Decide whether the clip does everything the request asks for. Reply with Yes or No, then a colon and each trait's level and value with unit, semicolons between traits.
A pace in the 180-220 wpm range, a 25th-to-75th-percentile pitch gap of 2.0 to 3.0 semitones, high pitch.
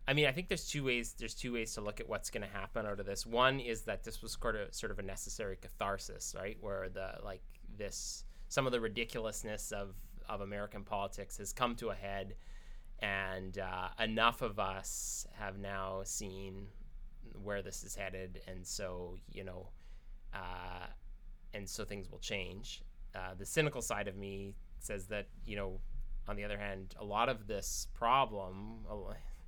No: average, 185 wpm; average, 2.7 semitones; low, 100 Hz